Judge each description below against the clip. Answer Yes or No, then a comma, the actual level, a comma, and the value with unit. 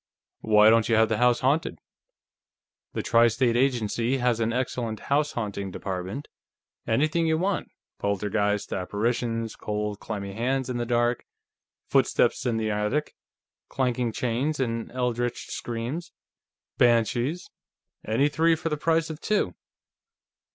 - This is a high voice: No, low, 120 Hz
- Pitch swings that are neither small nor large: Yes, average, 3.6 semitones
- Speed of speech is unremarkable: No, slow, 130 wpm